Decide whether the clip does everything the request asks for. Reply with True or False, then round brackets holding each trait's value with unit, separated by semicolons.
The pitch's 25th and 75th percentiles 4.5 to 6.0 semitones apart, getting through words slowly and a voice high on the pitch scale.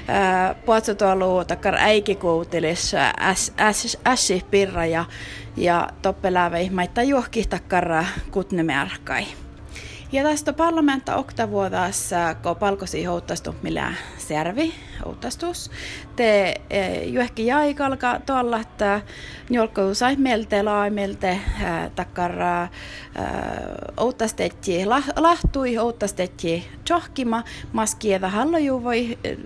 True (5.2 semitones; 85 wpm; 205 Hz)